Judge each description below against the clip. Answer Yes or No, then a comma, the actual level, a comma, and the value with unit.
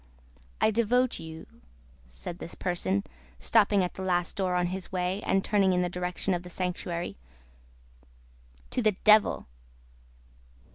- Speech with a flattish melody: Yes, narrow, 2.2 semitones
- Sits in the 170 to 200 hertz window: Yes, medium, 185 Hz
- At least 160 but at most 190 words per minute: No, average, 140 wpm